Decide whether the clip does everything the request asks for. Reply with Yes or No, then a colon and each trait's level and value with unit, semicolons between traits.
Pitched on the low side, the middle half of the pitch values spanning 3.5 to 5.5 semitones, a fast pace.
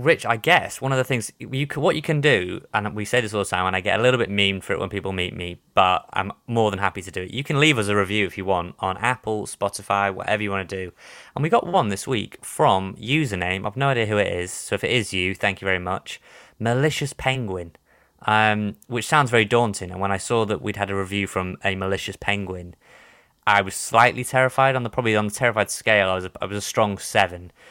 Yes: low, 105 Hz; average, 4.0 semitones; fast, 260 wpm